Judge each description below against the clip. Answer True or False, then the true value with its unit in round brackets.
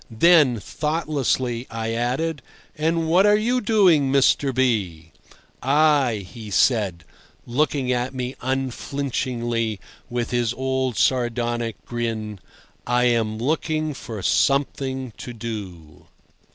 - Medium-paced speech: False (110 wpm)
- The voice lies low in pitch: True (125 Hz)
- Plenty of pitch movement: False (3.8 semitones)